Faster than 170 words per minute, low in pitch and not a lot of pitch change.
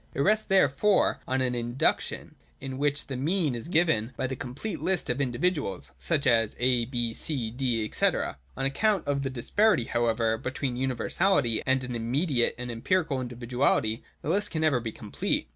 No: average, 180 wpm; low, 130 Hz; average, 4.5 semitones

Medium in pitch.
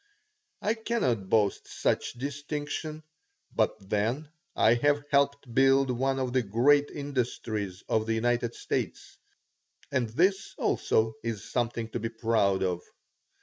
No: low, 120 Hz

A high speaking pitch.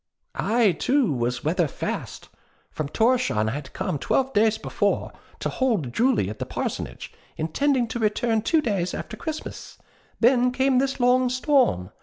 Yes: high, 230 Hz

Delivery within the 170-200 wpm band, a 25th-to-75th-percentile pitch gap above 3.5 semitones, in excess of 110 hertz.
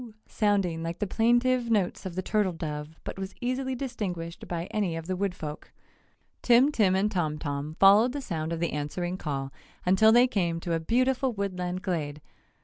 Yes: average, 180 wpm; average, 5.1 semitones; medium, 185 Hz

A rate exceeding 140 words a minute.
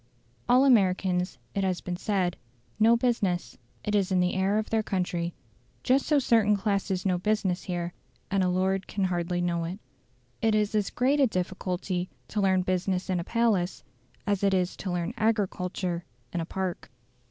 Yes: average, 175 wpm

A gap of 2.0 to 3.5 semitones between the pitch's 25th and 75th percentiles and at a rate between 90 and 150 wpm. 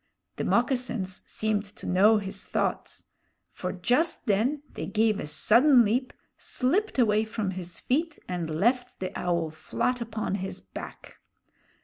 No: average, 4.9 semitones; average, 140 wpm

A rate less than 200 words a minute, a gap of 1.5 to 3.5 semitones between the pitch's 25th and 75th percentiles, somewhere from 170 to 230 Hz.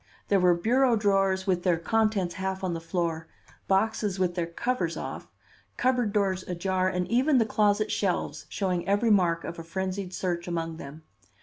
Yes: average, 175 wpm; average, 3.2 semitones; high, 190 Hz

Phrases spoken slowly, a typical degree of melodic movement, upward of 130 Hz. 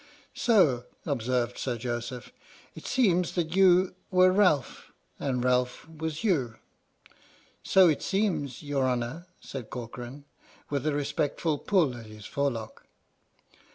No: slow, 130 wpm; wide, 6.0 semitones; medium, 140 Hz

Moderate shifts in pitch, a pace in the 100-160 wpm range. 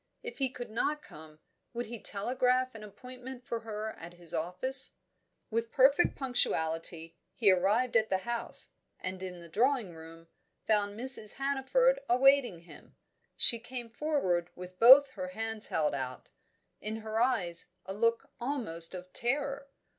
No: wide, 5.9 semitones; average, 150 wpm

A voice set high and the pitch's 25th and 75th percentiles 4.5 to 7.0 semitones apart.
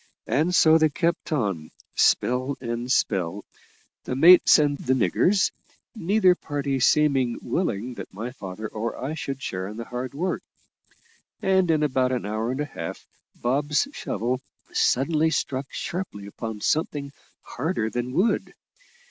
No: low, 130 Hz; average, 5.1 semitones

